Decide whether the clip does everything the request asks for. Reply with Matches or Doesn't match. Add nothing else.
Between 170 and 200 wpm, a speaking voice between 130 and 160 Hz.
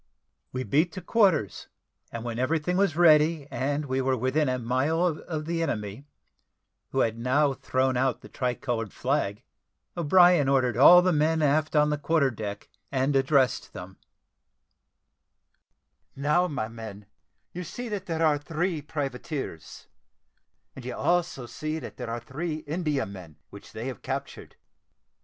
Doesn't match